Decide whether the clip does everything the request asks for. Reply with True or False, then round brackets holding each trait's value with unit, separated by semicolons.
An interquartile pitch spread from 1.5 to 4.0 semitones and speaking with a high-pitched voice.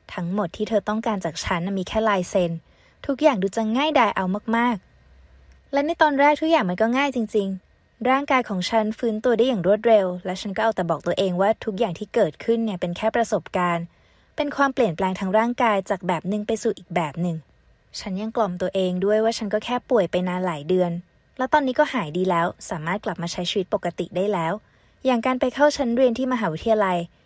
False (4.5 semitones; 210 Hz)